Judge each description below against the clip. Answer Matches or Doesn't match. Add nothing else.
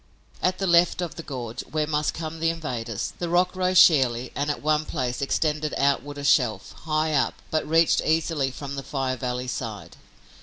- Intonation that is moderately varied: Matches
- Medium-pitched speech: Matches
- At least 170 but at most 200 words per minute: Matches